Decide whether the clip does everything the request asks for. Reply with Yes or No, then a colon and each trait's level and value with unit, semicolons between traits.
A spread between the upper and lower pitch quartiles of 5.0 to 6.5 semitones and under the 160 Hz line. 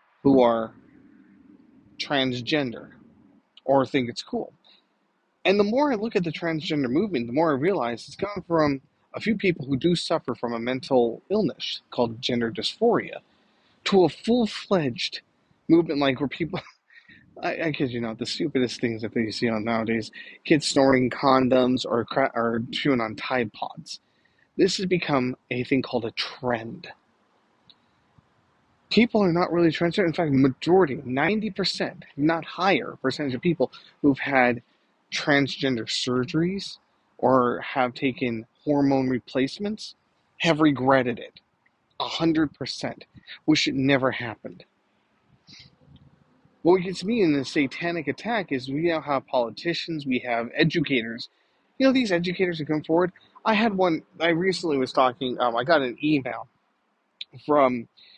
Yes: average, 5.3 semitones; medium, 140 Hz